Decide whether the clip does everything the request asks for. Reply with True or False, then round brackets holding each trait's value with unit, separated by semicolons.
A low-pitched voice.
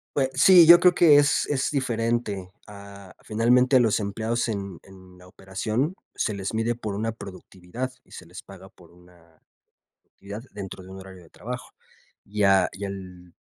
True (100 Hz)